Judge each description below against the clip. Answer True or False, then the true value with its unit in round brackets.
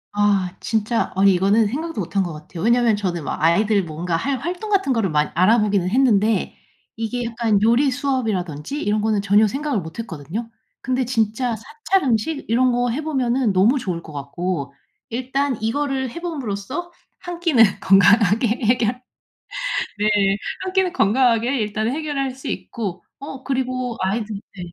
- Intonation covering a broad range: False (4.9 semitones)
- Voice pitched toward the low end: False (225 Hz)